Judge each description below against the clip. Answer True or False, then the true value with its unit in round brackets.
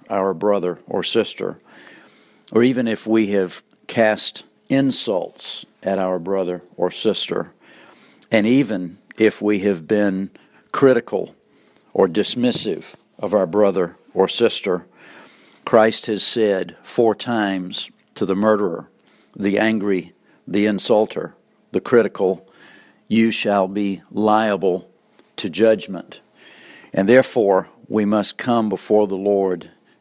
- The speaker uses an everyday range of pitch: False (2.3 semitones)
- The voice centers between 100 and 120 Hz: True (105 Hz)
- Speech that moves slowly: True (115 wpm)